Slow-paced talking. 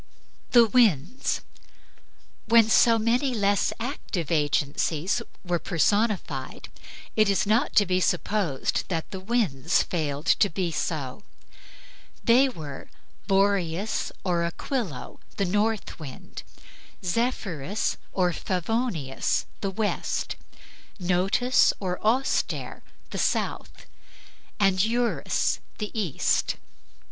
Yes: slow, 100 wpm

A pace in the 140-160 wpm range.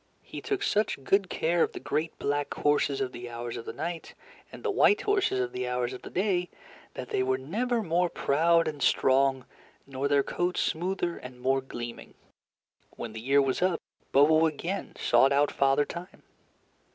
No: average, 185 wpm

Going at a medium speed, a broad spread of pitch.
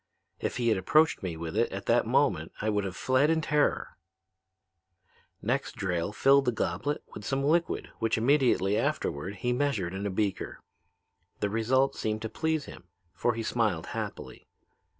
Yes: average, 170 wpm; wide, 5.9 semitones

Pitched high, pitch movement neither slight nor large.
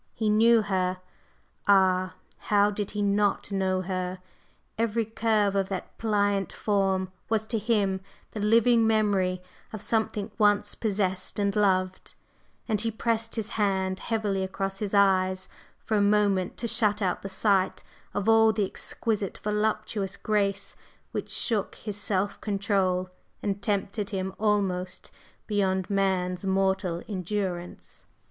No: high, 200 Hz; narrow, 2.0 semitones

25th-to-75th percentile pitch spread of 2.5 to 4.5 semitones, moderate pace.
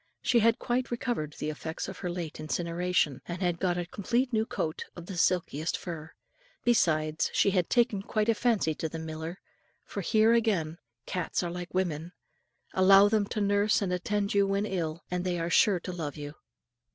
Yes: average, 3.9 semitones; average, 190 wpm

